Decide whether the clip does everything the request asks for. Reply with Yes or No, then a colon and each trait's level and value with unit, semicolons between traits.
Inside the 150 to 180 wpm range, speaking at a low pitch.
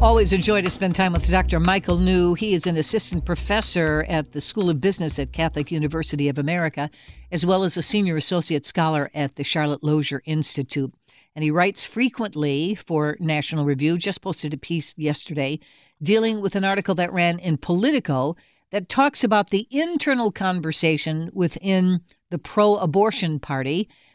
No: average, 170 wpm; medium, 170 Hz